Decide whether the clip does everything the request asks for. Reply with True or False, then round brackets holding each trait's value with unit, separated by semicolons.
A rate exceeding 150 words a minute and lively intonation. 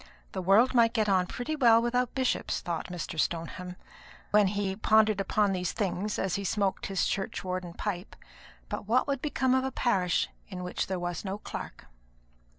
False (175 wpm; 4.1 semitones)